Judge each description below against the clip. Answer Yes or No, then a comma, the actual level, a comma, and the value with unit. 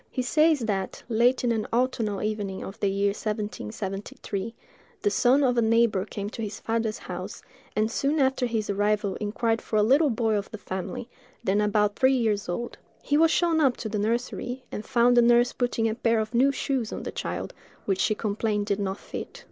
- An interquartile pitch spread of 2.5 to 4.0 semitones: Yes, average, 3.0 semitones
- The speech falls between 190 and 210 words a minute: Yes, fast, 205 wpm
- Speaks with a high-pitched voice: Yes, high, 225 Hz